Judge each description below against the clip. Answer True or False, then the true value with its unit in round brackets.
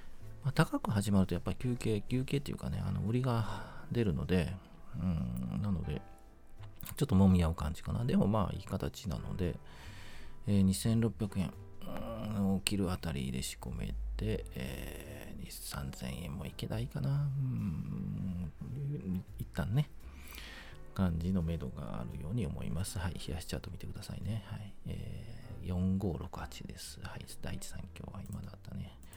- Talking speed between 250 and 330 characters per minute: True (280 characters per minute)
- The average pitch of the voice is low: True (100 Hz)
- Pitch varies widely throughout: False (4.4 semitones)